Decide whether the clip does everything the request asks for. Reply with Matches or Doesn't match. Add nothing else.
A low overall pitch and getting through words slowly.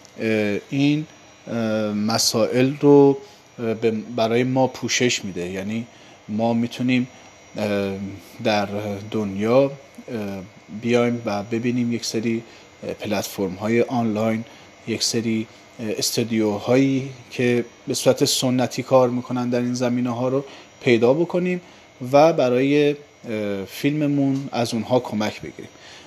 Matches